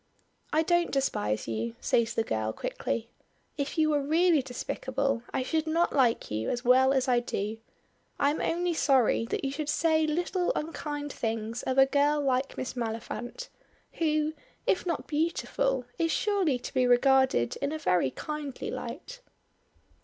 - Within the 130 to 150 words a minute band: No, average, 160 wpm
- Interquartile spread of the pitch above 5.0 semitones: No, average, 4.5 semitones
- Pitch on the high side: Yes, very high, 275 Hz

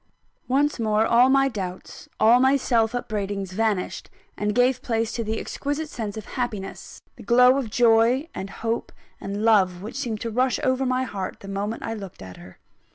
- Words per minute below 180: No, average, 185 wpm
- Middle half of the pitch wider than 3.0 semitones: Yes, average, 3.7 semitones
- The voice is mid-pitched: No, high, 225 Hz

